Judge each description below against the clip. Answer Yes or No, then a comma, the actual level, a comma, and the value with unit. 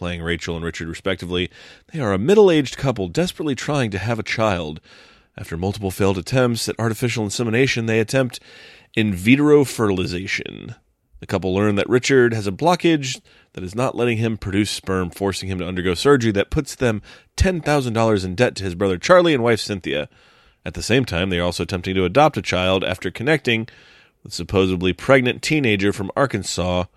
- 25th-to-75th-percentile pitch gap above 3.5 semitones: Yes, average, 5.3 semitones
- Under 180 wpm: No, average, 185 wpm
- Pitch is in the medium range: No, low, 105 Hz